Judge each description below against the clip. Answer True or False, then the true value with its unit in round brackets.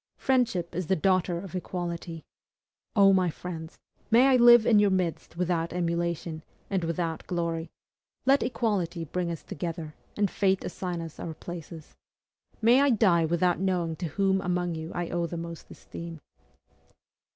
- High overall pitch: False (175 Hz)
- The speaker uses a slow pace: False (155 wpm)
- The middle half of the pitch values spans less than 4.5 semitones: True (2.5 semitones)